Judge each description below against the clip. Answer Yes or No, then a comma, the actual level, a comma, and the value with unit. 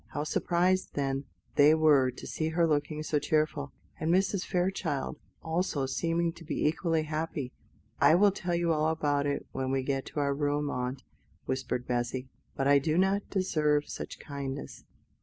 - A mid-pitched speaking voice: Yes, medium, 150 Hz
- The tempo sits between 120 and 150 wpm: No, average, 170 wpm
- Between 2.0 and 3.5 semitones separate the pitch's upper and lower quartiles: Yes, average, 3.1 semitones